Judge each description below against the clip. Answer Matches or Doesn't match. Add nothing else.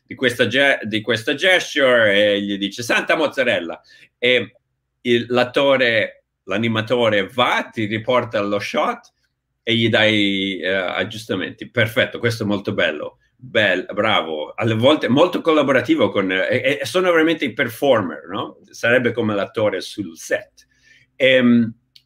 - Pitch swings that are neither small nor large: Matches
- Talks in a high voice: Doesn't match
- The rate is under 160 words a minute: Matches